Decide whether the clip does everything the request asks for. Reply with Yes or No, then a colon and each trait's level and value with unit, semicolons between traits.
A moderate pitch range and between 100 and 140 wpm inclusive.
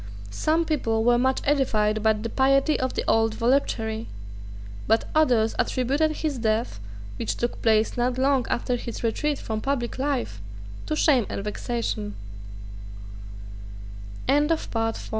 Yes: average, 3.9 semitones; slow, 135 wpm